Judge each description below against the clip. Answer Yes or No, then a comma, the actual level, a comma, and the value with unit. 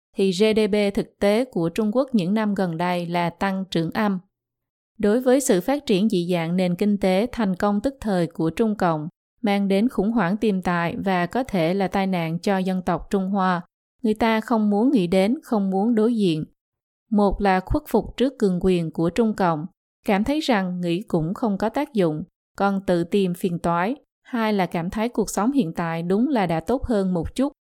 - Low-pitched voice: No, high, 200 Hz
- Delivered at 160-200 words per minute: No, average, 210 wpm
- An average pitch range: Yes, average, 3.7 semitones